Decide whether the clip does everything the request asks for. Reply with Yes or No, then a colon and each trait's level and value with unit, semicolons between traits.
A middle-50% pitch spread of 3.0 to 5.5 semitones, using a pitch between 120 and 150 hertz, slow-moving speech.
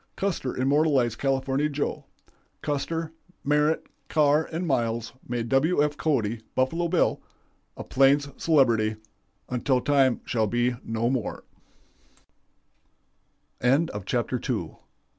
Yes: average, 3.8 semitones; low, 135 Hz; slow, 105 wpm